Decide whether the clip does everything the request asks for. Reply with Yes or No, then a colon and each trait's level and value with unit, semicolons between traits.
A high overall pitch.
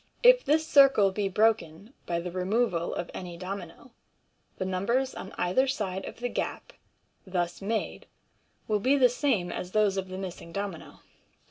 Yes: high, 195 Hz